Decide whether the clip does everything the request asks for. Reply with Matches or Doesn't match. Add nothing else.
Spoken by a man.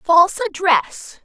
Doesn't match